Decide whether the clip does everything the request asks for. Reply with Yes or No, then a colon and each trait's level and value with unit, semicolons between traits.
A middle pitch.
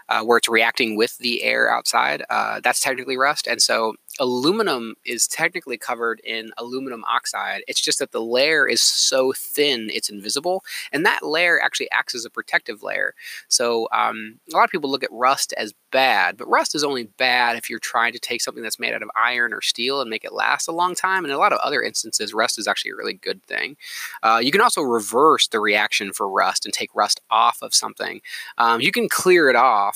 No: low, 125 Hz